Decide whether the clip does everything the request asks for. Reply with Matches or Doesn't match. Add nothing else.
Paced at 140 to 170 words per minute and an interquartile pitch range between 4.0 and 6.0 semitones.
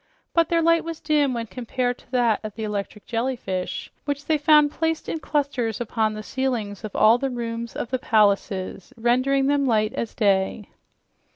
Doesn't match